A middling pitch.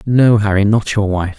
No: low, 105 Hz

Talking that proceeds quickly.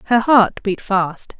No: average, 170 wpm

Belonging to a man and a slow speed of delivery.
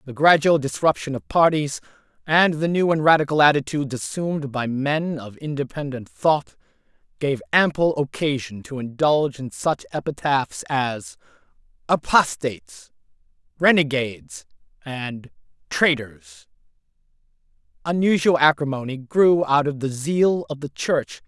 Yes: male; slow, 120 wpm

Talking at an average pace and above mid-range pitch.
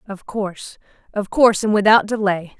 Yes: average, 160 wpm; high, 205 Hz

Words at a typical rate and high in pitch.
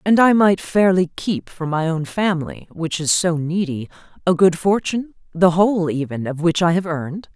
No: average, 190 wpm; medium, 170 Hz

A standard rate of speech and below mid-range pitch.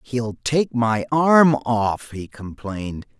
No: slow, 130 wpm; low, 120 Hz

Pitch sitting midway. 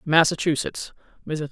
Yes: medium, 155 Hz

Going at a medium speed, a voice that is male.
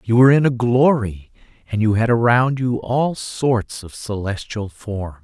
Yes: average, 170 wpm; male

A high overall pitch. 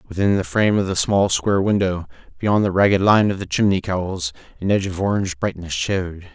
No: very low, 95 Hz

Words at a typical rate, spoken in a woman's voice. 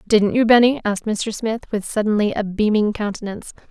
Yes: average, 180 wpm; female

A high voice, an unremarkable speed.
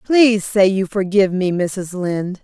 Yes: high, 195 Hz; average, 170 wpm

